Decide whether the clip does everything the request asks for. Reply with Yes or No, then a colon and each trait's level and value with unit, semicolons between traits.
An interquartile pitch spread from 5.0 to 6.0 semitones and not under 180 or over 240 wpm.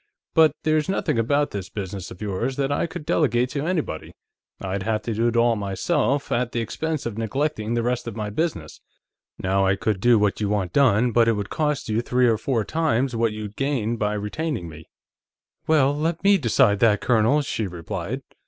Yes: average, 5.3 semitones; average, 200 wpm